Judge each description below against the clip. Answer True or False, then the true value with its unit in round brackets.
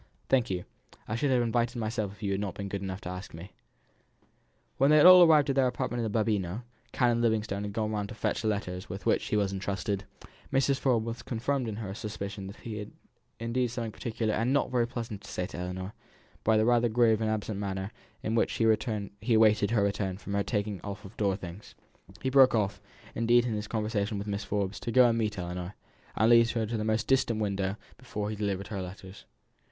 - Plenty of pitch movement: False (2.8 semitones)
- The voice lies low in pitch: True (110 Hz)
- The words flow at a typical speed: False (225 wpm)